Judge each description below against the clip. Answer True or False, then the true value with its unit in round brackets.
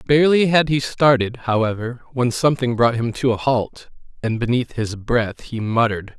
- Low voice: True (120 Hz)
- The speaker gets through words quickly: False (175 wpm)